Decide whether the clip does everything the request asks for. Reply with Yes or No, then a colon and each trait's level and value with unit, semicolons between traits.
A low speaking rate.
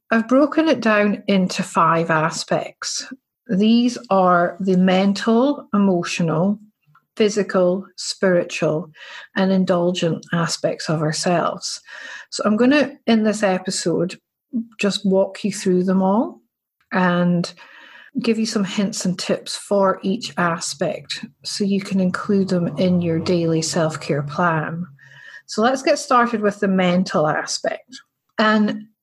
Yes: slow, 125 wpm